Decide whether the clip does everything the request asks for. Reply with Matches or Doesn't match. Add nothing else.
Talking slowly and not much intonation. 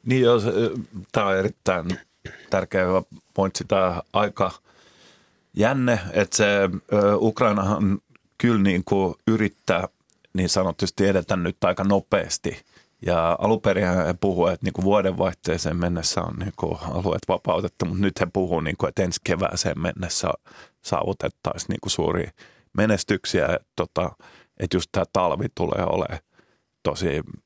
Doesn't match